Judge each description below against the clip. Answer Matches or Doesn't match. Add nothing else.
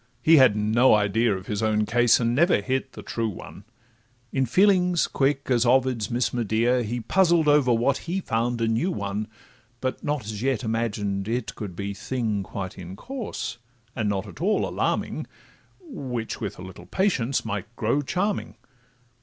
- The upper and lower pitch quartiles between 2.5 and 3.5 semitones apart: Doesn't match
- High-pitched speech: Doesn't match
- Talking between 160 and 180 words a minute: Matches